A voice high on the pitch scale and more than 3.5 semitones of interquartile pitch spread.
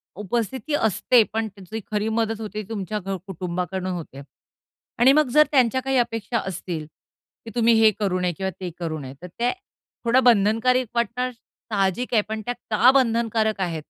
Yes: high, 220 Hz; average, 4.0 semitones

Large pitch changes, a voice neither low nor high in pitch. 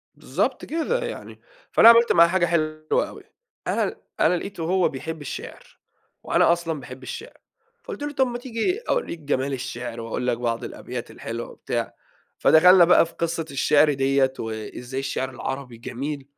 Yes: wide, 5.9 semitones; medium, 150 Hz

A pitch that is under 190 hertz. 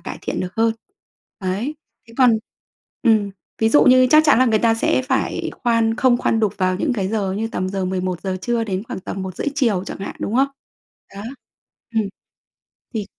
No: high, 225 Hz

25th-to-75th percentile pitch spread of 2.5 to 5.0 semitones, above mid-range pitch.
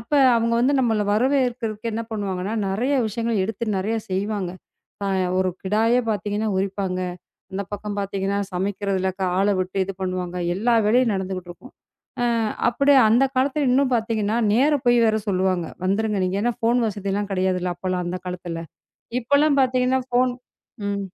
Yes: average, 4.0 semitones; high, 210 Hz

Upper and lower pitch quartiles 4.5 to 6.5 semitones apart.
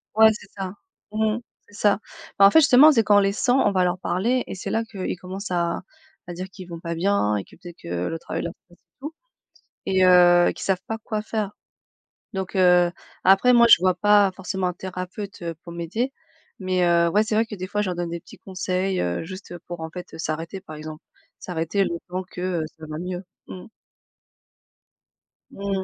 No: average, 2.8 semitones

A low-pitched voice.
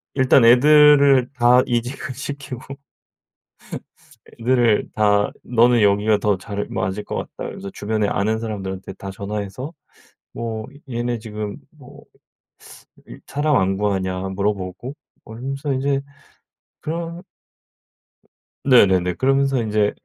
Yes: low, 115 Hz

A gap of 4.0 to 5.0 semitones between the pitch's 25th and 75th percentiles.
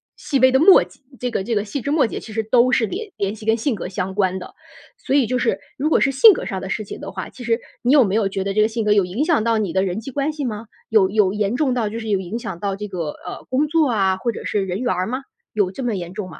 Yes: average, 4.6 semitones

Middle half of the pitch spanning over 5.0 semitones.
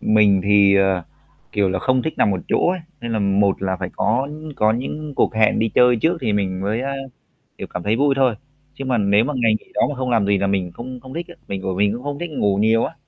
No: average, 4.6 semitones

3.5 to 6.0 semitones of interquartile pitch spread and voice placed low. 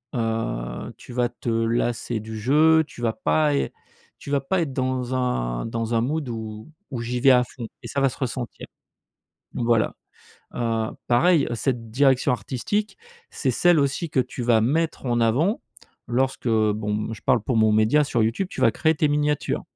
Yes: average, 3.8 semitones; low, 125 Hz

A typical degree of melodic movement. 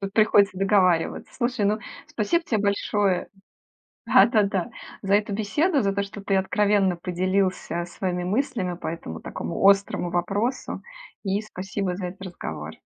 No: narrow, 2.3 semitones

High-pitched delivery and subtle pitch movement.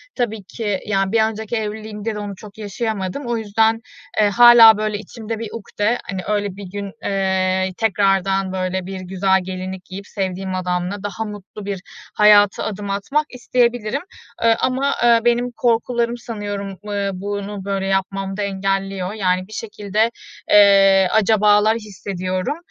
Yes: high, 205 Hz; narrow, 2.3 semitones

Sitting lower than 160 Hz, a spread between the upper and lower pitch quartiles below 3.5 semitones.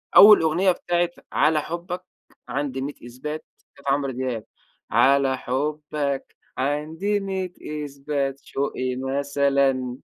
Yes: medium, 140 Hz; average, 3.0 semitones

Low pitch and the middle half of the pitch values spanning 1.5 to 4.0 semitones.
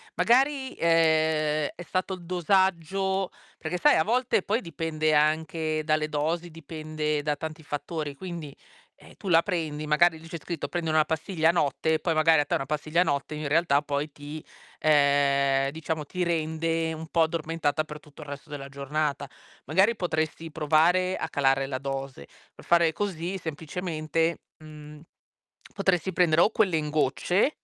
No: medium, 160 Hz; narrow, 2.4 semitones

